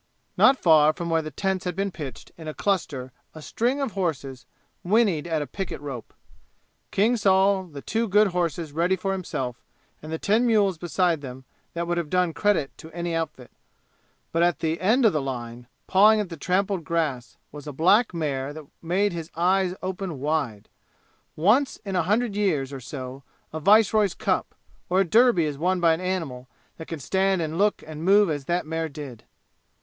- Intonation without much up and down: No, average, 4.4 semitones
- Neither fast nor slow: Yes, average, 190 wpm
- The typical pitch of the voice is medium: Yes, medium, 170 Hz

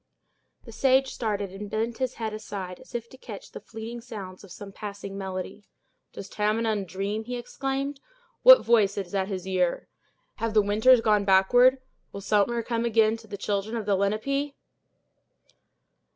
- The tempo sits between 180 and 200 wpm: No, average, 165 wpm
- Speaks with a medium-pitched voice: No, high, 215 Hz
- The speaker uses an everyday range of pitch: Yes, average, 3.1 semitones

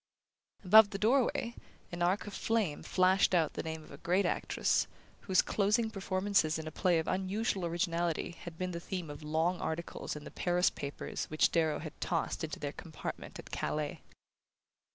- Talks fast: No, average, 175 wpm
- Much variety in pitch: No, average, 3.4 semitones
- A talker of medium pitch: Yes, medium, 175 Hz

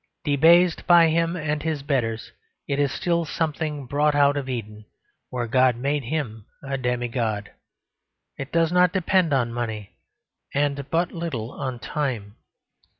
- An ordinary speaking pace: Yes, average, 145 wpm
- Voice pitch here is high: No, medium, 140 Hz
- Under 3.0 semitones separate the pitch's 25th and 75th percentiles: No, average, 4.9 semitones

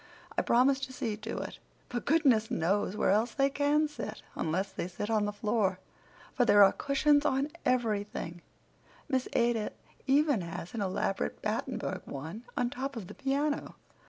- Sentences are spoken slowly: No, average, 165 wpm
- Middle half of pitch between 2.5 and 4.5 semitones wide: No, average, 5.1 semitones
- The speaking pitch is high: Yes, high, 230 Hz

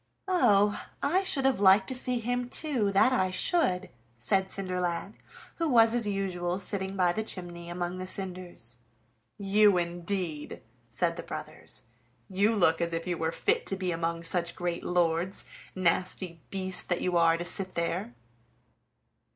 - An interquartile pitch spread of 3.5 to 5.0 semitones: No, average, 2.9 semitones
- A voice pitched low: No, medium, 185 Hz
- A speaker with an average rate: Yes, average, 160 wpm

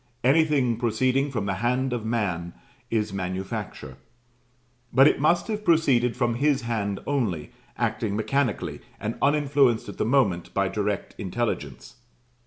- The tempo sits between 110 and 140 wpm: Yes, slow, 135 wpm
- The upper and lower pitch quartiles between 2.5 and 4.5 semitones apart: No, average, 5.0 semitones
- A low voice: Yes, low, 120 Hz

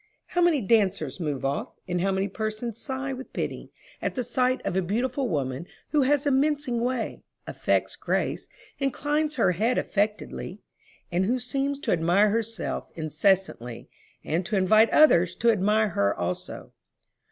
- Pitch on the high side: Yes, high, 215 Hz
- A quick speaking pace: No, average, 155 wpm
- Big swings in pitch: Yes, wide, 6.2 semitones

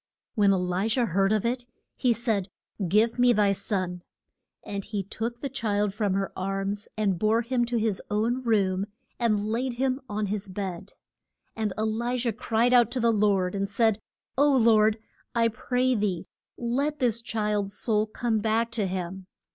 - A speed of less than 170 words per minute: No, average, 175 wpm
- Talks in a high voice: Yes, high, 215 Hz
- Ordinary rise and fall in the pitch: Yes, average, 3.0 semitones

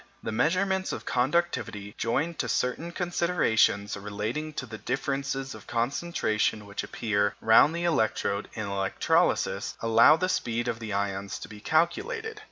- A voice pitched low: Yes, low, 120 Hz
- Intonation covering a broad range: Yes, wide, 8.1 semitones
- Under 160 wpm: Yes, average, 145 wpm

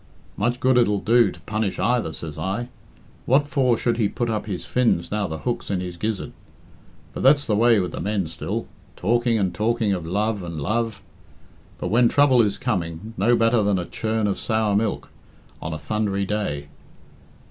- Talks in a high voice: No, low, 105 Hz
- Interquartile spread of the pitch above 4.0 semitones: No, average, 3.5 semitones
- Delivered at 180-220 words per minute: Yes, average, 190 wpm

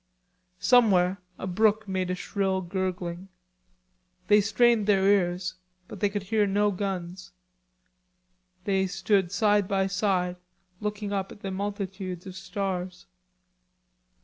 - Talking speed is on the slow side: Yes, slow, 120 wpm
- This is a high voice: Yes, high, 195 Hz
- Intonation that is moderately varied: No, narrow, 1.9 semitones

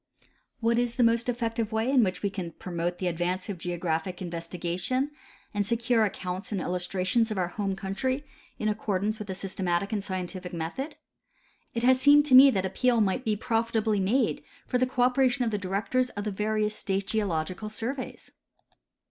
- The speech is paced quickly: No, average, 180 wpm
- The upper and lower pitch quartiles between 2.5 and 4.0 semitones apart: No, average, 4.4 semitones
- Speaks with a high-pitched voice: Yes, high, 210 Hz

